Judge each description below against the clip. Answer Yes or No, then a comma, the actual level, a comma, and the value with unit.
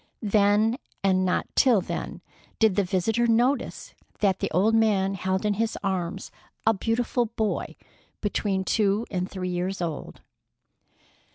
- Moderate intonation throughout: Yes, average, 3.0 semitones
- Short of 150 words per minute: Yes, average, 140 wpm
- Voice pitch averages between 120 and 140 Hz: No, high, 200 Hz